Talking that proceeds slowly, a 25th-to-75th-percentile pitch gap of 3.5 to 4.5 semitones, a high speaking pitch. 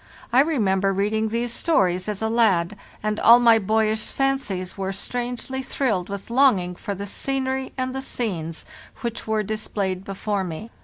No: average, 160 wpm; average, 4.1 semitones; high, 215 Hz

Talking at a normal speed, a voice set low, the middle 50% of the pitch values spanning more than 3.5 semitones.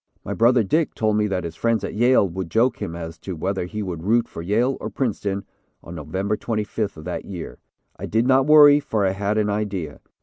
No: fast, 225 wpm; low, 105 Hz; average, 3.9 semitones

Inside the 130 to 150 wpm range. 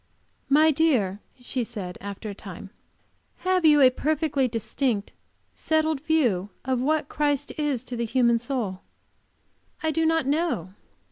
Yes: average, 140 wpm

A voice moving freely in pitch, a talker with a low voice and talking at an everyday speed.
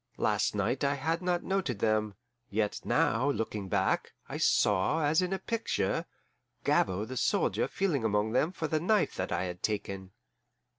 Yes: wide, 7.8 semitones; low, 125 Hz; average, 165 wpm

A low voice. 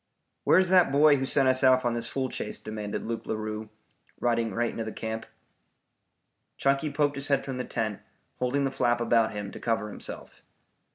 Yes: low, 120 Hz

